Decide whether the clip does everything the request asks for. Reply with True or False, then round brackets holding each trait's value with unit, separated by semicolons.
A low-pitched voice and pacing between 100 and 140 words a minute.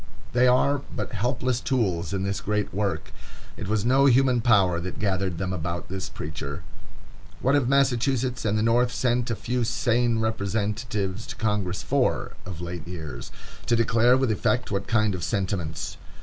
False (110 Hz; 165 wpm)